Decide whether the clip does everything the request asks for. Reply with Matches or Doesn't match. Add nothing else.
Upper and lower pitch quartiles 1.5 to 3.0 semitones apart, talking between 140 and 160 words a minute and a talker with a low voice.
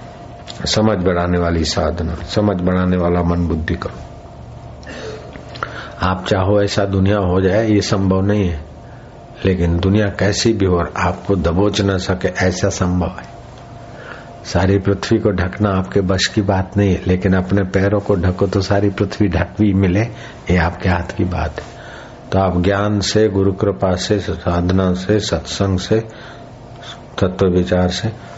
Matches